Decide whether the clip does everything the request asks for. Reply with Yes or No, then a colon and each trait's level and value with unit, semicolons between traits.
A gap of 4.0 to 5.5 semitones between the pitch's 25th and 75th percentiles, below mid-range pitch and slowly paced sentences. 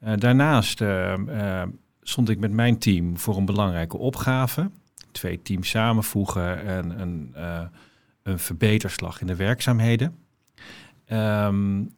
Yes: average, 4.5 semitones; low, 105 Hz; slow, 125 wpm